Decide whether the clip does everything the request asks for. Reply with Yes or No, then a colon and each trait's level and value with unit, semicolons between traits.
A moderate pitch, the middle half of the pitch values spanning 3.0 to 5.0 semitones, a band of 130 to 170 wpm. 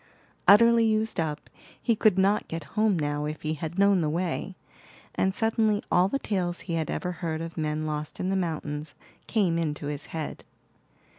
No: medium, 175 Hz; average, 4.5 semitones; average, 180 wpm